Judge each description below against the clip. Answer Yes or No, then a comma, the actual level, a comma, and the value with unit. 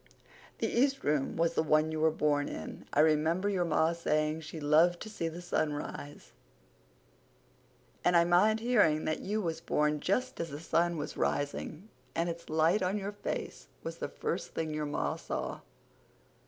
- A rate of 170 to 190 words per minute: Yes, average, 175 wpm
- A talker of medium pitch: Yes, medium, 165 Hz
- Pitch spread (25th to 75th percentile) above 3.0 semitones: No, narrow, 2.6 semitones